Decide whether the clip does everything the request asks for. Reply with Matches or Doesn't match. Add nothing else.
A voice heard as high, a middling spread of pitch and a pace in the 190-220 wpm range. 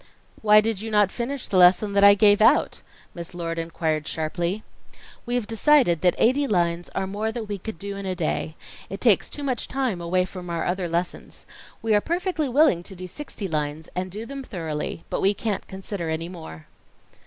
Matches